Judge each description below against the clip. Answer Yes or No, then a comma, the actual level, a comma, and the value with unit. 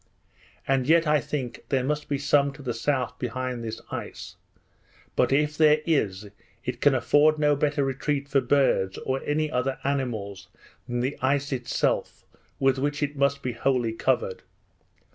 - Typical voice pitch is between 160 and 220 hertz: No, low, 135 Hz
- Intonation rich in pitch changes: No, average, 2.7 semitones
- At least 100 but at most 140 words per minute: No, average, 160 wpm